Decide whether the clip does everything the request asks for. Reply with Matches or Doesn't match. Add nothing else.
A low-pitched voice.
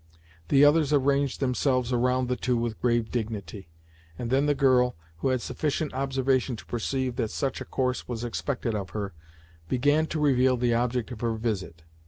Matches